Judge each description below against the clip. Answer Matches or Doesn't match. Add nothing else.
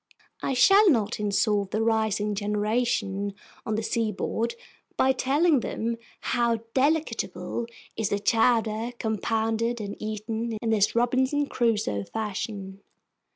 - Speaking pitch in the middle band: Doesn't match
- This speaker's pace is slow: Matches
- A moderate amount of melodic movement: Doesn't match